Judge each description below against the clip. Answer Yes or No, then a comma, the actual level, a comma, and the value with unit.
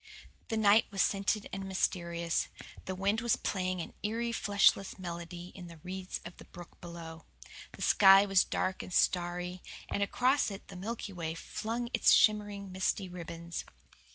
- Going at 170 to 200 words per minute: No, average, 160 wpm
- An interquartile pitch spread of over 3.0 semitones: No, average, 2.7 semitones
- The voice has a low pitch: No, high, 190 Hz